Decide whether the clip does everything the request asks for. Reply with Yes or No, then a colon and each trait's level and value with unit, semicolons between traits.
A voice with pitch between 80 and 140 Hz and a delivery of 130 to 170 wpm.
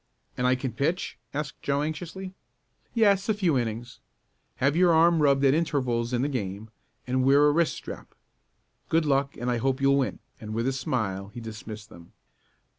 No: low, 135 Hz; average, 185 wpm